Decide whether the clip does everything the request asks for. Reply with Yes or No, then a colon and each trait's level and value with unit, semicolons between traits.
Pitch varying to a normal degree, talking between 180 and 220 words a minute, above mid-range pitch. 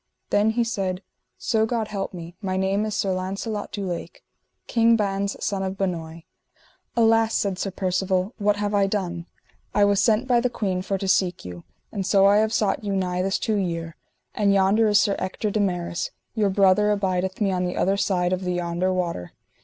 No: narrow, 2.2 semitones; average, 200 wpm; high, 195 Hz